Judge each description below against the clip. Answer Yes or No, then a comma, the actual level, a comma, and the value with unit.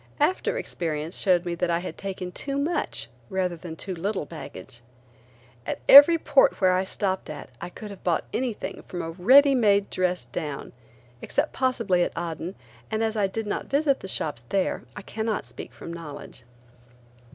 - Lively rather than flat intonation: No, average, 4.8 semitones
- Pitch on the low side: No, high, 190 Hz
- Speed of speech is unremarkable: Yes, average, 175 wpm